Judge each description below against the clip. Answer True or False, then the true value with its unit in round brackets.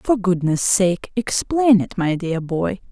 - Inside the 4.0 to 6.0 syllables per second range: False (3.6 syllables/s)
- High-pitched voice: True (195 Hz)